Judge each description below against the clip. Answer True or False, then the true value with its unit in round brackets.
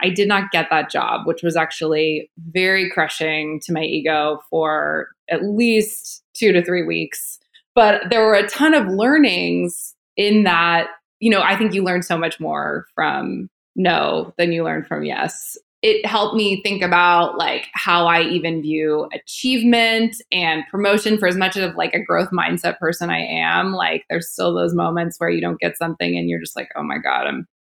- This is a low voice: False (175 Hz)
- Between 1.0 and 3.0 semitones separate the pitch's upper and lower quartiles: False (4.8 semitones)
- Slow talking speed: False (190 wpm)